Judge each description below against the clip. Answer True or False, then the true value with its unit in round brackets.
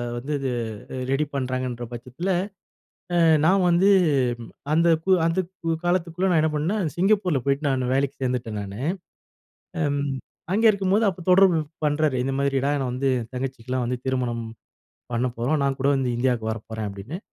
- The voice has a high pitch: False (135 Hz)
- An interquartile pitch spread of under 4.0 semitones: False (5.1 semitones)